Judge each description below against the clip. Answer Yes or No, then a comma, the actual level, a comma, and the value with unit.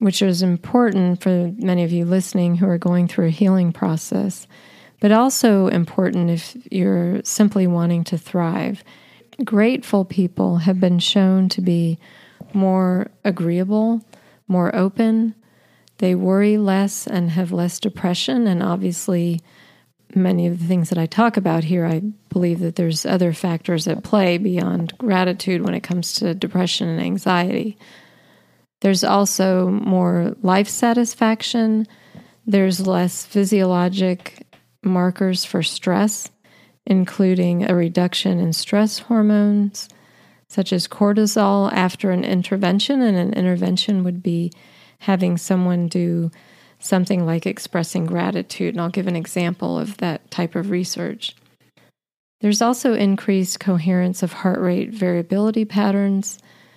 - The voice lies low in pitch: No, medium, 185 Hz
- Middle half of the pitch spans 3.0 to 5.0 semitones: No, narrow, 2.6 semitones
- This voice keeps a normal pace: No, slow, 130 wpm